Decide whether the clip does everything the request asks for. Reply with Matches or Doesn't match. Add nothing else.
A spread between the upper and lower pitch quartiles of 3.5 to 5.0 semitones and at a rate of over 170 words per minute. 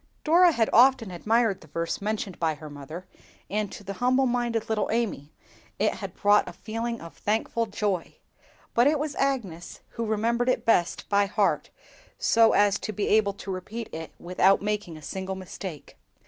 Matches